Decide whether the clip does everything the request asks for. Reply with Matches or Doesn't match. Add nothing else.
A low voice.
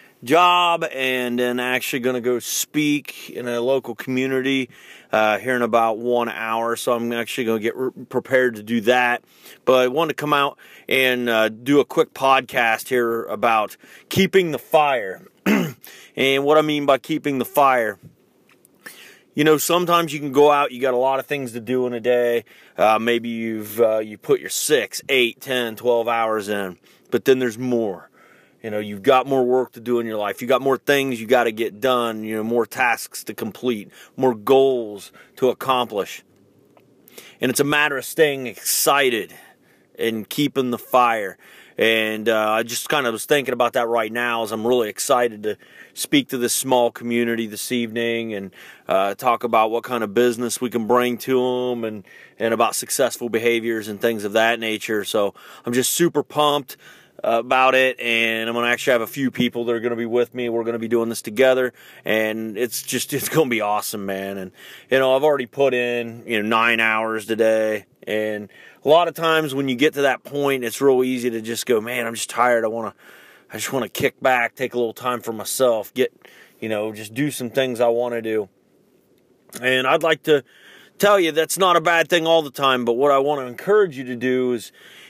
Matches